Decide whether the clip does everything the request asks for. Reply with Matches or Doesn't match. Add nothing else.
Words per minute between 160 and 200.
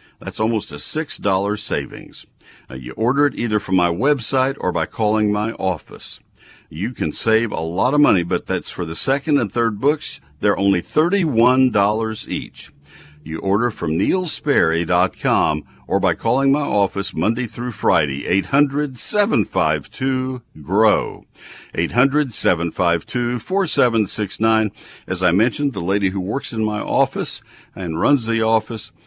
Doesn't match